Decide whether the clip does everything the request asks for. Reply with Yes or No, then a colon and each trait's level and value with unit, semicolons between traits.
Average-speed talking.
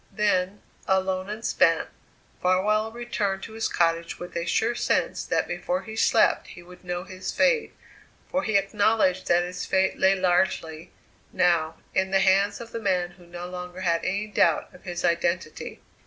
Yes: average, 170 wpm